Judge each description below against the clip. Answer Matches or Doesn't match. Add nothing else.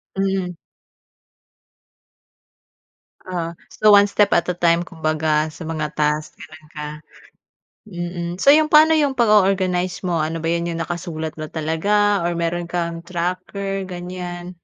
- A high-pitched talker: Doesn't match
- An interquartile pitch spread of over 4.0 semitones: Doesn't match